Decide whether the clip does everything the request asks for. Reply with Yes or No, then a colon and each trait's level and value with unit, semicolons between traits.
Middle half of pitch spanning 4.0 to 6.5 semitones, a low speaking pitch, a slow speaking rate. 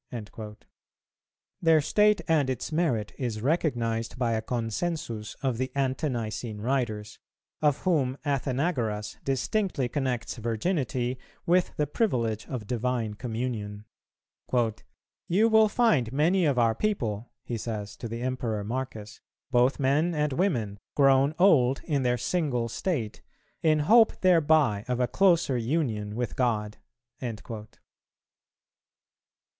Yes: average, 5.2 semitones; low, 125 Hz; slow, 125 wpm